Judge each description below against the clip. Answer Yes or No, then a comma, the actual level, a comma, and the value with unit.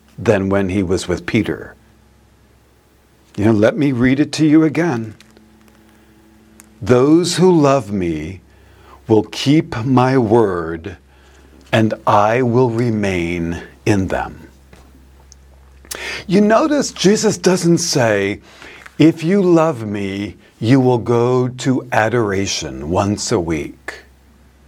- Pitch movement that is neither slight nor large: No, wide, 7.5 semitones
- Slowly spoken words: Yes, slow, 110 wpm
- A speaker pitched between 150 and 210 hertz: No, low, 110 Hz